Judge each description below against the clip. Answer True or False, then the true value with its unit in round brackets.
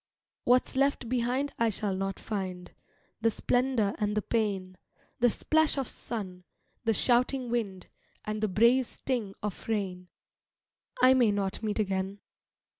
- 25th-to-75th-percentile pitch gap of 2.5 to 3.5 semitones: False (4.0 semitones)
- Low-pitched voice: False (215 Hz)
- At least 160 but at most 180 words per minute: False (140 wpm)